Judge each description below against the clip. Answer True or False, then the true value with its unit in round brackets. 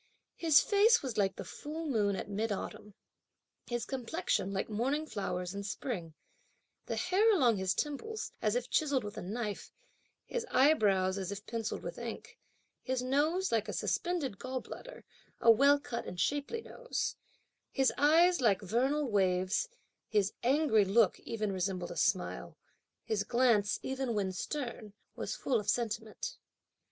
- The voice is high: True (235 Hz)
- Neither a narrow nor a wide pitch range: False (6.2 semitones)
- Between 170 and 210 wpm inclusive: False (150 wpm)